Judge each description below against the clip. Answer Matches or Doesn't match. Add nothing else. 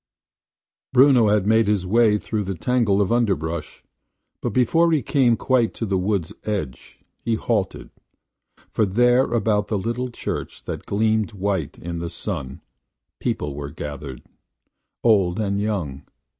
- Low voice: Matches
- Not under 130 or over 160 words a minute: Matches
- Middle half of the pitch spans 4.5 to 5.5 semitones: Doesn't match